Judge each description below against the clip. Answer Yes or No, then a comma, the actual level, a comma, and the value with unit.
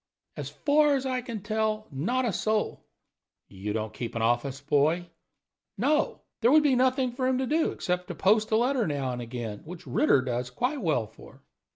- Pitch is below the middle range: No, high, 205 Hz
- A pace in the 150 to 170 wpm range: No, average, 195 wpm